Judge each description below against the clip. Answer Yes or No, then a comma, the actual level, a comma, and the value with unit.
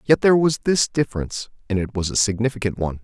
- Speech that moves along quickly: Yes, fast, 220 wpm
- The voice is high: No, low, 115 Hz